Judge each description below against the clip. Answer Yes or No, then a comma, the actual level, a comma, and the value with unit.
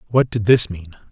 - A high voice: No, low, 105 Hz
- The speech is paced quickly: Yes, fast, 215 wpm